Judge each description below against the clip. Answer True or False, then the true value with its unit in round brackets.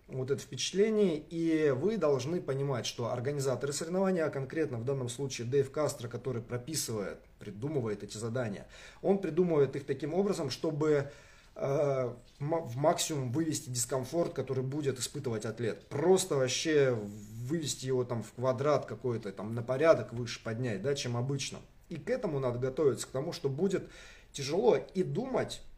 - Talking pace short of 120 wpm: False (155 wpm)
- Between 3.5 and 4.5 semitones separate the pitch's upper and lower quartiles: True (4.2 semitones)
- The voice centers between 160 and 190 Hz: False (140 Hz)